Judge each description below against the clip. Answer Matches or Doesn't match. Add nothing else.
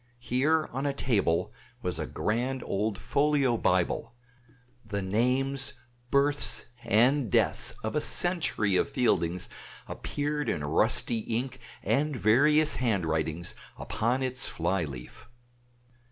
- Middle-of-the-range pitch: Doesn't match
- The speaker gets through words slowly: Matches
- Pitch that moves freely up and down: Matches